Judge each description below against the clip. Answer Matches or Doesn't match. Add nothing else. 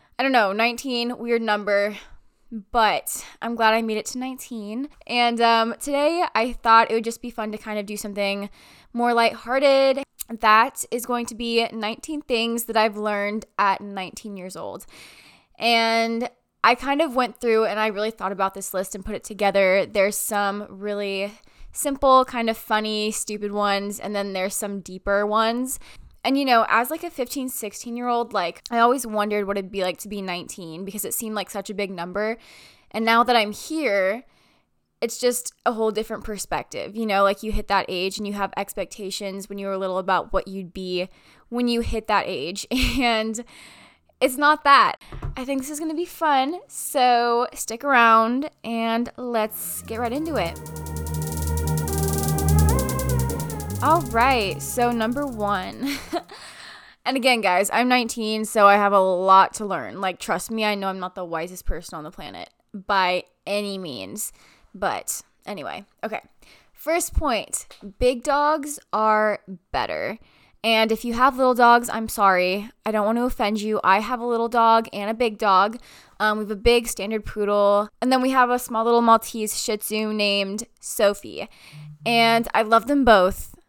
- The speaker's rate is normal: Matches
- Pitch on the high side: Matches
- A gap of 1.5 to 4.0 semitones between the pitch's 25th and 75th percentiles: Matches